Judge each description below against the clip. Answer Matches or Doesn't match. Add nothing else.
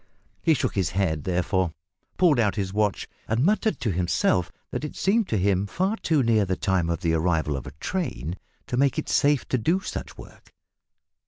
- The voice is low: Matches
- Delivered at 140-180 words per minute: Doesn't match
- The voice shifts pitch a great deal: Matches